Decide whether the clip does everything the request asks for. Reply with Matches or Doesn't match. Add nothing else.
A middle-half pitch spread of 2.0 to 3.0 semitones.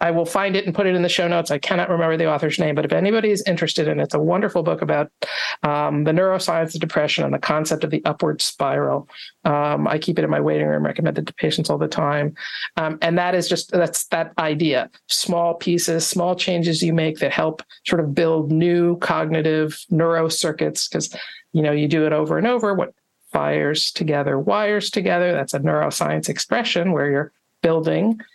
Matches